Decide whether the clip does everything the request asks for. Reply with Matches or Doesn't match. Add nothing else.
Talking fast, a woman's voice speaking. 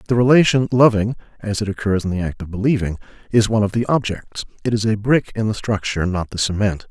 Doesn't match